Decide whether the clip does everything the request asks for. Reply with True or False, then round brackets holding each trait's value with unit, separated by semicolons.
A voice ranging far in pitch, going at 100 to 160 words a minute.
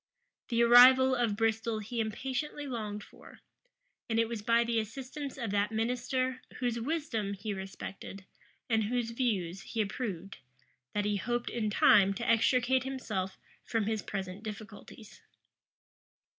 False (3.1 semitones; 140 wpm)